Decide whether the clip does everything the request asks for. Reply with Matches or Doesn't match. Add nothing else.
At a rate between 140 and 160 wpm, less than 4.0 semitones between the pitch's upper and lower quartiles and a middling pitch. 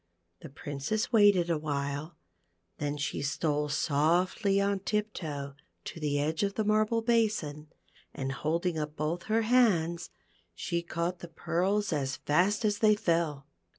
Doesn't match